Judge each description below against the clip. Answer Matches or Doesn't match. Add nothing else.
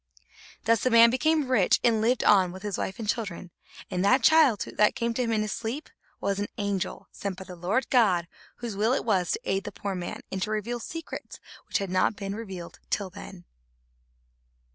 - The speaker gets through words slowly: Doesn't match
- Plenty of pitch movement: Doesn't match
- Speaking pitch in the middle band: Doesn't match